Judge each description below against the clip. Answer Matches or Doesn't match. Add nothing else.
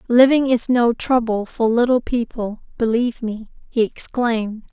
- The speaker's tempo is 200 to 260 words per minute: Doesn't match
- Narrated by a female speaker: Matches